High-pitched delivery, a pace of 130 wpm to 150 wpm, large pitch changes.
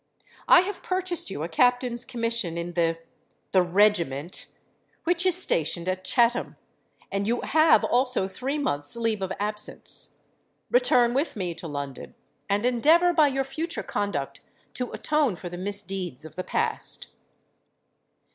Yes: high, 215 Hz; average, 140 wpm; wide, 7.2 semitones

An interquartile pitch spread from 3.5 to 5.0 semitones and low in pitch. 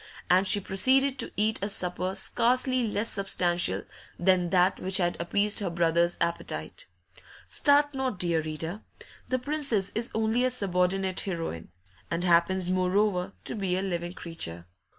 No: average, 3.9 semitones; high, 190 Hz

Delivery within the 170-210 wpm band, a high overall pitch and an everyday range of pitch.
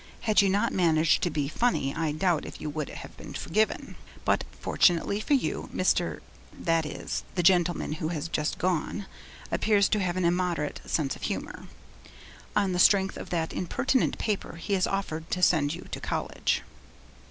No: average, 175 wpm; medium, 175 Hz; average, 3.5 semitones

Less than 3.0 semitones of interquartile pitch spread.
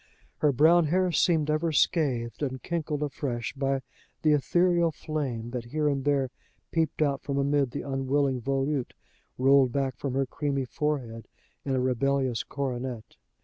Yes: narrow, 2.5 semitones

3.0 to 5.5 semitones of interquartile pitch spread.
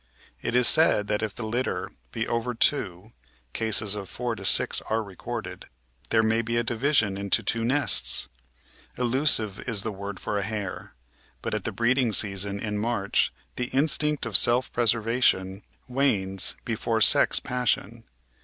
Yes: average, 3.4 semitones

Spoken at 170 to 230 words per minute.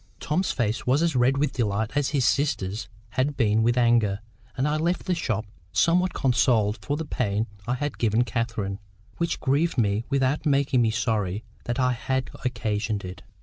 Yes: average, 180 wpm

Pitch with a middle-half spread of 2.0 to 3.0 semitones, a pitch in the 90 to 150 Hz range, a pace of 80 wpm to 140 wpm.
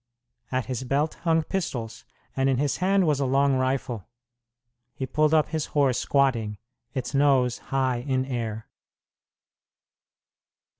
Yes: narrow, 2.6 semitones; low, 135 Hz; slow, 135 wpm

